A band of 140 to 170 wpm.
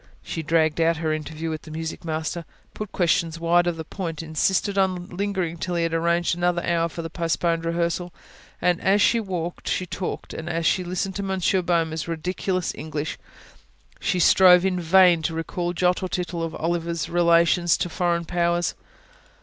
No: average, 180 wpm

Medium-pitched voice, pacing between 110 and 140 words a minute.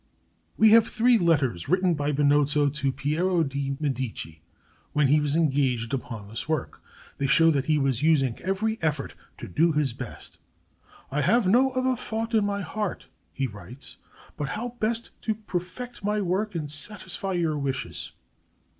No: medium, 155 Hz; average, 165 wpm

